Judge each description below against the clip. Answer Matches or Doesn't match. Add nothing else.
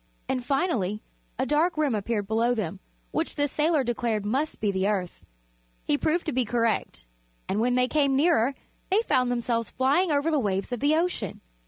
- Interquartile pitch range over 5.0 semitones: Matches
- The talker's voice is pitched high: Matches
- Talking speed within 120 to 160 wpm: Doesn't match